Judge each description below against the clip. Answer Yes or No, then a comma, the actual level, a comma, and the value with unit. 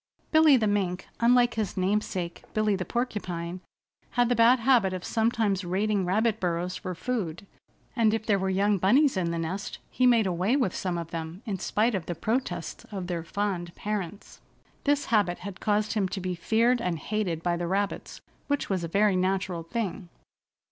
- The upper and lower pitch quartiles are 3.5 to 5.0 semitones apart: Yes, average, 3.8 semitones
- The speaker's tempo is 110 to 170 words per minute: No, average, 185 wpm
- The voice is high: Yes, high, 195 Hz